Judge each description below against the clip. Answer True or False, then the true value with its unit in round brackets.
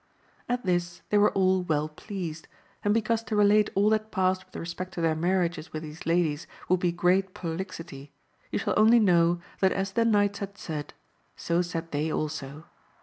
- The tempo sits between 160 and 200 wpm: True (185 wpm)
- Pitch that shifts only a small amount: False (3.4 semitones)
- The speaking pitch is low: False (180 Hz)